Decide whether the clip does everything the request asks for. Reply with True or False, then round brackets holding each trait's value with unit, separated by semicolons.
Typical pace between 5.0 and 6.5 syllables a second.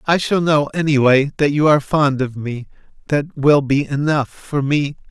False (4.6 syllables/s)